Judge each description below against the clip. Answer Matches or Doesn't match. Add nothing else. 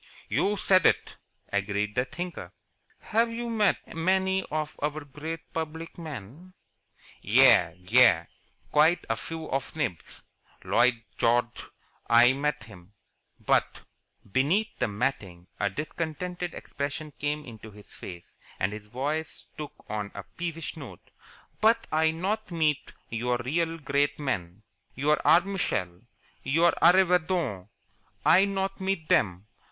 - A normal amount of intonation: Doesn't match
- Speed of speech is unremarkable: Doesn't match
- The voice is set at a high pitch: Doesn't match